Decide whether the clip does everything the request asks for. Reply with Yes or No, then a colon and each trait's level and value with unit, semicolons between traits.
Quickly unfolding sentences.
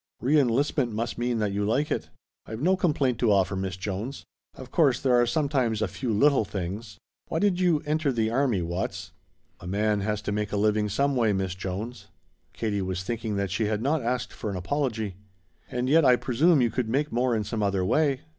Yes: fast, 215 wpm